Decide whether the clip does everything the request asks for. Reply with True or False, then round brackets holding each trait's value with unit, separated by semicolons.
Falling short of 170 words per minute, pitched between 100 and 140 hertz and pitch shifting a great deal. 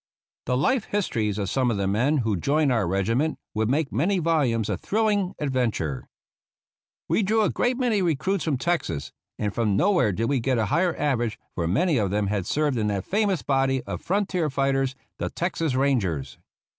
False (185 wpm; 135 Hz; 8.0 semitones)